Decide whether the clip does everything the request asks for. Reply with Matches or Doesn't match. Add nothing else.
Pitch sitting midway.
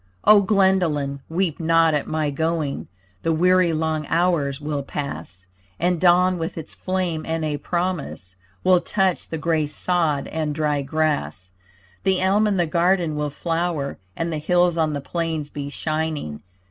Matches